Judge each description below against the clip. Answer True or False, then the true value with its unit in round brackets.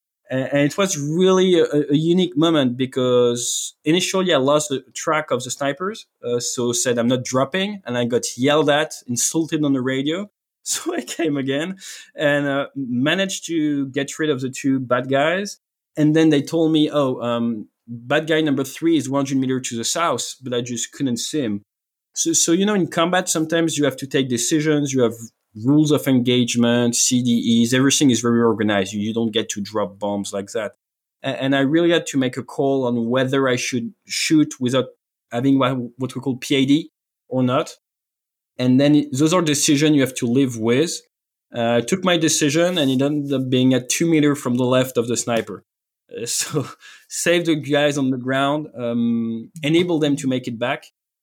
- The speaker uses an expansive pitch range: False (4.1 semitones)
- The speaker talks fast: False (190 wpm)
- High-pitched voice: False (135 Hz)